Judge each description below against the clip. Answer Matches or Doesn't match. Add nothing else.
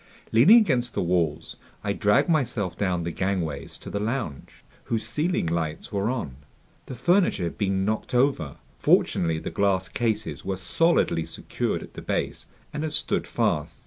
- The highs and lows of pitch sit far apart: Matches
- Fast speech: Doesn't match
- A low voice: Matches